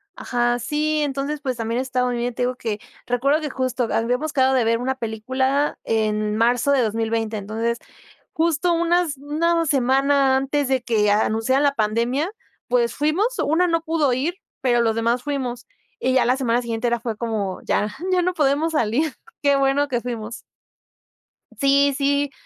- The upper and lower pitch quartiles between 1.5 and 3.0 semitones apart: No, average, 3.6 semitones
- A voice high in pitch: Yes, very high, 260 Hz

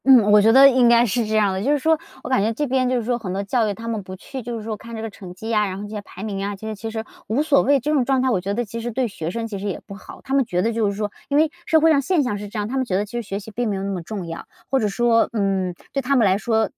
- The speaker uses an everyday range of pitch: Yes, average, 3.9 semitones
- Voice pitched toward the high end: Yes, high, 220 Hz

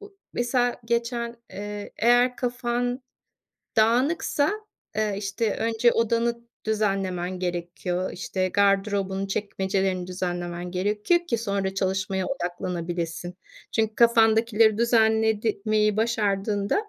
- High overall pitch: Yes, high, 210 Hz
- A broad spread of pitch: No, average, 3.5 semitones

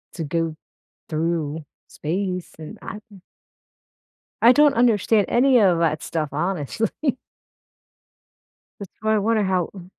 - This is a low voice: No, medium, 185 Hz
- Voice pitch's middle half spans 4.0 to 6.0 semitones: Yes, average, 5.1 semitones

